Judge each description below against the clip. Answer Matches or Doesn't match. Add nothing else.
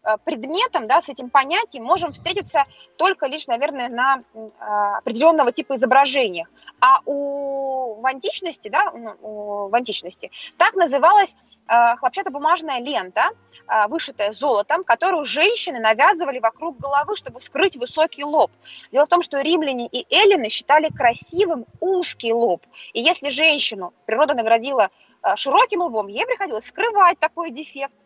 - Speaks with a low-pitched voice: Doesn't match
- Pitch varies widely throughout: Matches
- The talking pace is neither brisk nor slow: Matches